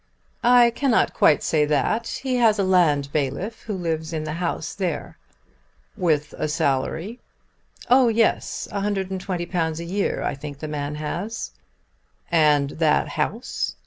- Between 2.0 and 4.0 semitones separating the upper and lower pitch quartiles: No, average, 5.3 semitones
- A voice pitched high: No, medium, 170 Hz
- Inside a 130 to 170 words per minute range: Yes, average, 140 wpm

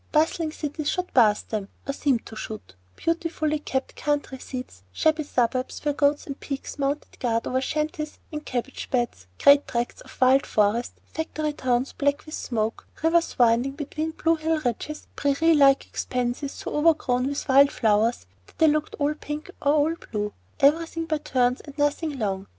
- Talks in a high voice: Yes, very high, 285 Hz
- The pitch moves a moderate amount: Yes, average, 3.7 semitones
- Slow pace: No, average, 170 wpm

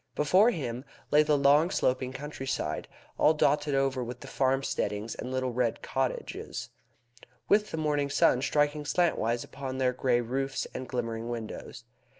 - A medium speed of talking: Yes, average, 150 wpm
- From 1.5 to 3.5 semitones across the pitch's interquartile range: Yes, average, 2.8 semitones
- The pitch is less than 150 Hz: Yes, low, 135 Hz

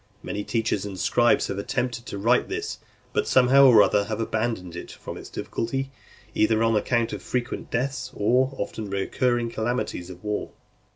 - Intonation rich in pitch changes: No, average, 3.3 semitones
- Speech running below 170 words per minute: No, average, 175 wpm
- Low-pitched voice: Yes, low, 115 Hz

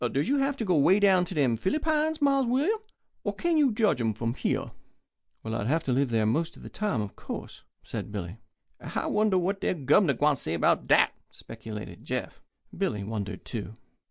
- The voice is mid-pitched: Yes, medium, 155 Hz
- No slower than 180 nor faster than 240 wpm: Yes, average, 195 wpm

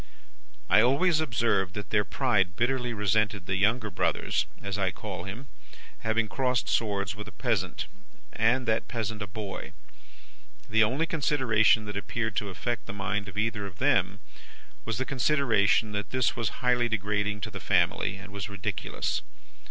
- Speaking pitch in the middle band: No, low, 110 Hz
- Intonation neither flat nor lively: Yes, average, 3.2 semitones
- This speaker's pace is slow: No, average, 160 wpm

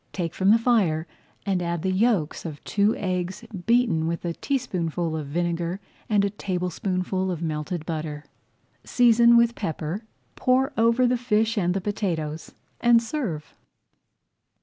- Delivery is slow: No, average, 145 wpm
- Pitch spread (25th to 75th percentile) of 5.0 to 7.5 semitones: Yes, wide, 5.5 semitones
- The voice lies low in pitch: No, medium, 185 Hz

